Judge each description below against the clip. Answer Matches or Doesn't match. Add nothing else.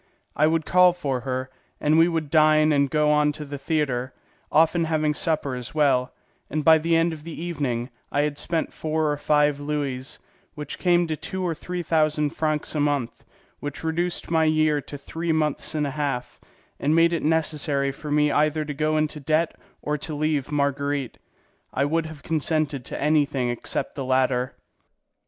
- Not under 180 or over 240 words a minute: Matches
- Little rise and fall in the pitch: Matches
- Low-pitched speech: Doesn't match